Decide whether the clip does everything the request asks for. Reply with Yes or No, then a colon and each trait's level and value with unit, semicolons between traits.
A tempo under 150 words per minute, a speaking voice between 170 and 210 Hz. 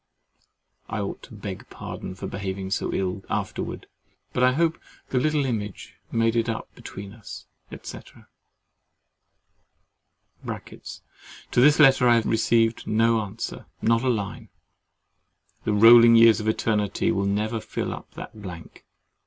No: slow, 135 wpm; low, 115 Hz